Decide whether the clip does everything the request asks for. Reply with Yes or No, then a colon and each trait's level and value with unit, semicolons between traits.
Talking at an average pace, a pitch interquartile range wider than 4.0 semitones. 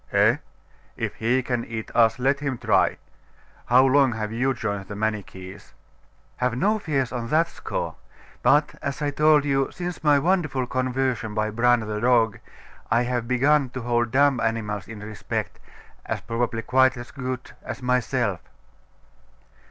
No: average, 155 wpm; average, 3.1 semitones